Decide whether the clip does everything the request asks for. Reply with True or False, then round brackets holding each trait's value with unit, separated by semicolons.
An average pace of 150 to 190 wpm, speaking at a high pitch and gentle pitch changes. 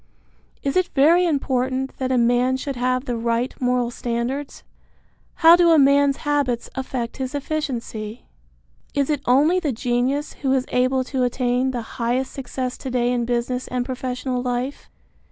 True (160 wpm; 255 Hz; 2.1 semitones)